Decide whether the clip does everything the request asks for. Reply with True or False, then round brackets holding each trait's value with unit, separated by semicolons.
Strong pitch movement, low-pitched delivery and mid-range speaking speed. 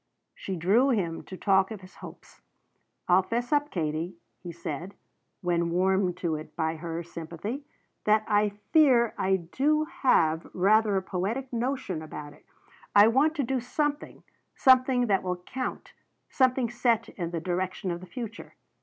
False (6.1 semitones; 195 Hz; 160 wpm)